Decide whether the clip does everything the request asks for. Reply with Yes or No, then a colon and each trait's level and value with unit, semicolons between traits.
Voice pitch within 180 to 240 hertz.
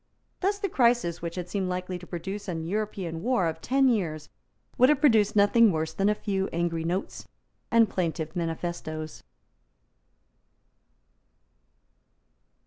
Yes: medium, 185 Hz